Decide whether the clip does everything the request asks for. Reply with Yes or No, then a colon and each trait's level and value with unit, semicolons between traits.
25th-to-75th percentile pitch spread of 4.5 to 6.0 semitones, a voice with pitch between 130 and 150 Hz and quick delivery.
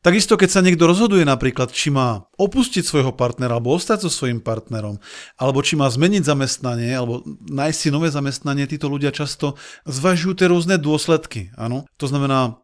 Yes: average, 5.1 semitones; medium, 140 Hz; fast, 170 wpm